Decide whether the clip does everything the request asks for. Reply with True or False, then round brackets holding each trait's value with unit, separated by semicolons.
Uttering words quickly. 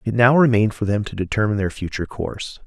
True (225 wpm)